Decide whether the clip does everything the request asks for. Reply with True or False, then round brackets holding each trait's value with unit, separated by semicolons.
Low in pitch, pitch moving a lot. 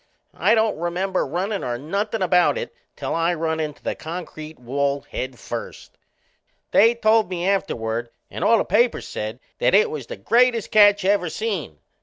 False (180 Hz; 6.2 semitones)